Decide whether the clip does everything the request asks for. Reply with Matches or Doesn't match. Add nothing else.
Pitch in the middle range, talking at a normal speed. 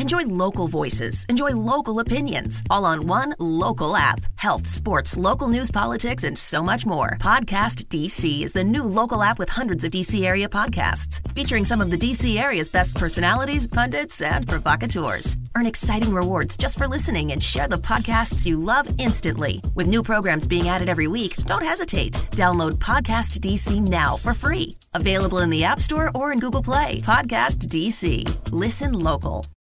Matches